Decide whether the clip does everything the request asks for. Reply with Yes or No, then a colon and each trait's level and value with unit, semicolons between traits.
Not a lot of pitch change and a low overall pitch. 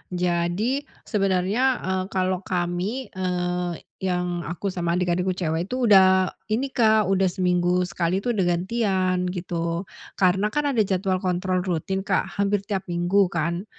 No: narrow, 2.1 semitones; medium, 185 Hz